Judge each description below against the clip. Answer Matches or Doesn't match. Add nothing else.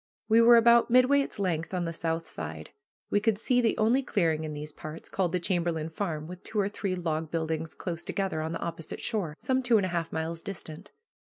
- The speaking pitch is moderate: Matches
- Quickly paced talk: Matches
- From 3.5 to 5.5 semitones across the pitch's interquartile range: Matches